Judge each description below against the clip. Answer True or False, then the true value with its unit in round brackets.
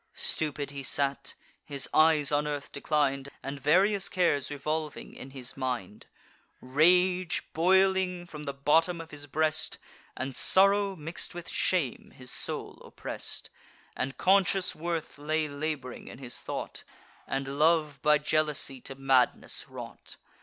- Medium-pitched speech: True (150 Hz)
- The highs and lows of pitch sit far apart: False (3.6 semitones)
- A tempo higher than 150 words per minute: False (135 wpm)